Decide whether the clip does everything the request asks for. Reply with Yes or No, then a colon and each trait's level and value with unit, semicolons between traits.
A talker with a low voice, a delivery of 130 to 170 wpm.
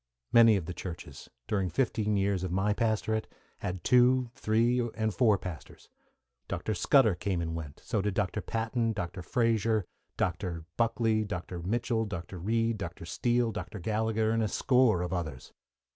Yes: low, 105 Hz; average, 160 wpm